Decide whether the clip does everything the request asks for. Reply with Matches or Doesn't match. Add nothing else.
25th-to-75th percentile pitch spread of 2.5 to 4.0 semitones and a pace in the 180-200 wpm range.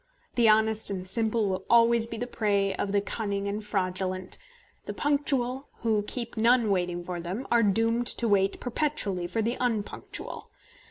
Doesn't match